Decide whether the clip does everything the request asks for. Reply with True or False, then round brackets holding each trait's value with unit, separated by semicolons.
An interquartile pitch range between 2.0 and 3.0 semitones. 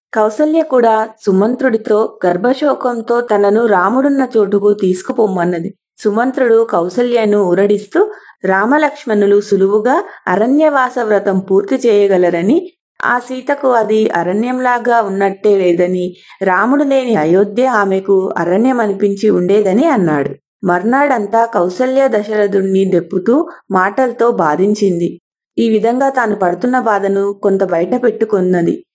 False (4.3 semitones)